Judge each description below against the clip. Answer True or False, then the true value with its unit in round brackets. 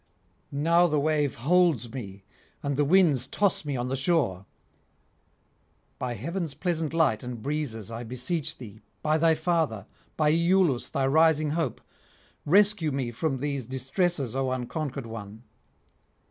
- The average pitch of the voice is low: False (145 Hz)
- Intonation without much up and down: False (4.8 semitones)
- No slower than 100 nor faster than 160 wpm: True (140 wpm)